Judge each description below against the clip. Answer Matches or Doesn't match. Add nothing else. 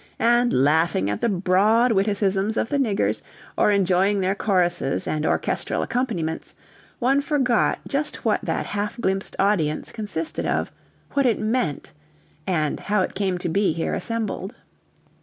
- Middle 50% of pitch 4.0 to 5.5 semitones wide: Matches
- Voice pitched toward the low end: Doesn't match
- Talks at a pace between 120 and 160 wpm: Matches